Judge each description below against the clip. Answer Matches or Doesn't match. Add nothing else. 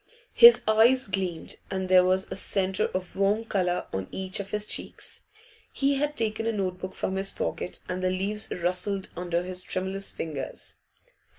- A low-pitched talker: Doesn't match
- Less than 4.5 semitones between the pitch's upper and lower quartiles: Matches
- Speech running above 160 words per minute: Matches